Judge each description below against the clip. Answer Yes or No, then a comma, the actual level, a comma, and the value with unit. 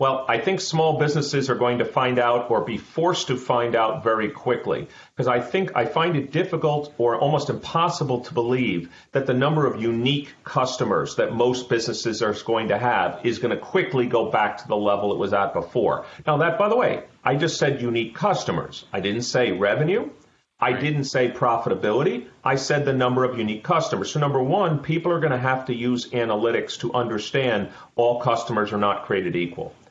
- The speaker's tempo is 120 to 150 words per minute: No, average, 200 wpm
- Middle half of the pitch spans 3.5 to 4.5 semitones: Yes, average, 3.9 semitones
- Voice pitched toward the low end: Yes, low, 125 Hz